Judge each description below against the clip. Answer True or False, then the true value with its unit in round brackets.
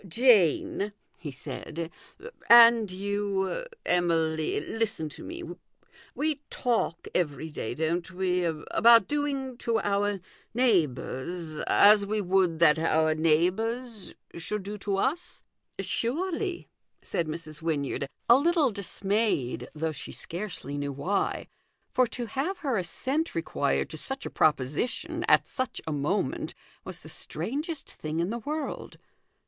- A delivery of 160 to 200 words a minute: False (140 wpm)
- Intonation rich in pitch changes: True (6.9 semitones)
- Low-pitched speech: False (195 Hz)